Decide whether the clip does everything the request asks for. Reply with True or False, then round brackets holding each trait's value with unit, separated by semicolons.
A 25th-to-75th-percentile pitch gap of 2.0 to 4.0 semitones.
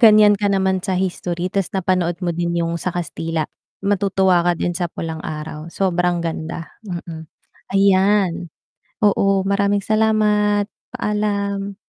True (2.8 semitones)